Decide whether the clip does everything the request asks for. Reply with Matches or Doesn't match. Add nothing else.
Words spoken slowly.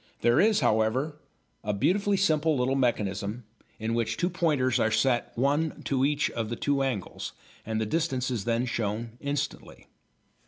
Doesn't match